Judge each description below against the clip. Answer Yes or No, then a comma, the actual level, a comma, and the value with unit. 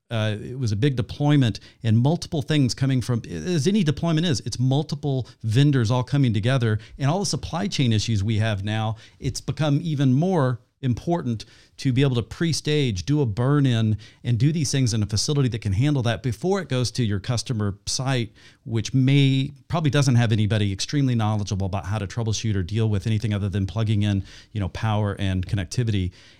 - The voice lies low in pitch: Yes, low, 120 Hz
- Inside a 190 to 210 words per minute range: Yes, average, 195 wpm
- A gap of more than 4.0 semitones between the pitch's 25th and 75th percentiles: Yes, average, 4.5 semitones